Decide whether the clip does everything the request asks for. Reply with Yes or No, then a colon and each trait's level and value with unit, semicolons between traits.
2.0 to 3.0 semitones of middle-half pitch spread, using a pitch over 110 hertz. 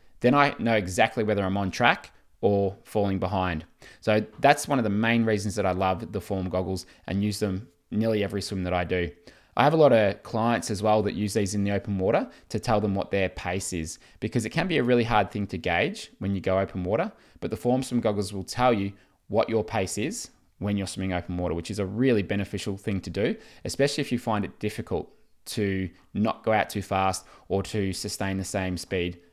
No: narrow, 2.5 semitones; low, 100 Hz